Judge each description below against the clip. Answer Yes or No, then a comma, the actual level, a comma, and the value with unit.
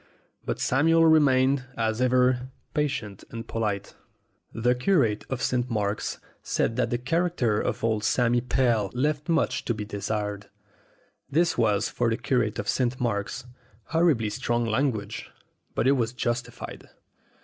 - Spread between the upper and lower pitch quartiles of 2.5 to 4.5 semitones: Yes, average, 3.3 semitones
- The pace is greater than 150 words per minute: No, average, 140 wpm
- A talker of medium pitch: No, low, 120 Hz